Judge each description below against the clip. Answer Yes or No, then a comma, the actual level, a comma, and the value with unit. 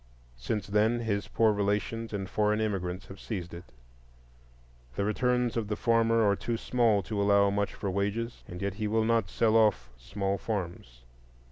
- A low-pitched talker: Yes, low, 105 Hz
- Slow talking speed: No, average, 170 wpm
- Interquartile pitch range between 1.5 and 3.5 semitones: Yes, narrow, 2.4 semitones